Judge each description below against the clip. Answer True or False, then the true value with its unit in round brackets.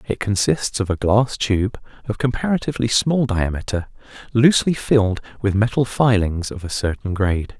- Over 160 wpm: False (150 wpm)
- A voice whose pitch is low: True (110 Hz)